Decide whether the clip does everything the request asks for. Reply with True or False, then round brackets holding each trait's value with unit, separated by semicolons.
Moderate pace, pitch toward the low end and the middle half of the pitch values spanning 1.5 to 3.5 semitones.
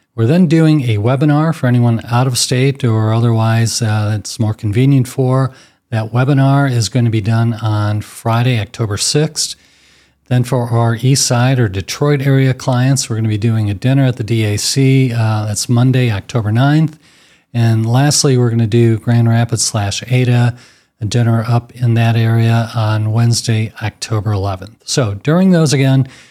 True (170 wpm; 115 Hz; 2.9 semitones)